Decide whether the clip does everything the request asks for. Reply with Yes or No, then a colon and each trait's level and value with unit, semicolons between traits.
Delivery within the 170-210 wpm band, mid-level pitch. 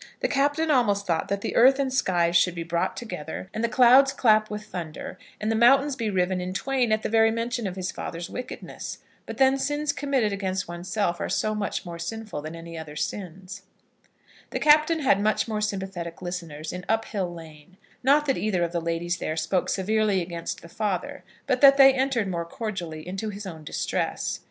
No: average, 200 wpm; high, 200 Hz